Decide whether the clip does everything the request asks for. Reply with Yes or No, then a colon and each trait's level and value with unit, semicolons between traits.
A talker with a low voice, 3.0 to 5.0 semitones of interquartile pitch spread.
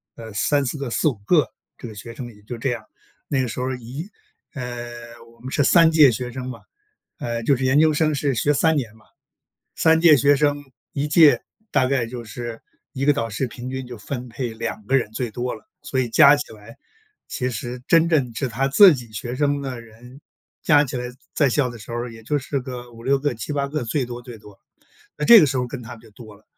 Yes: low, 125 Hz; average, 3.3 semitones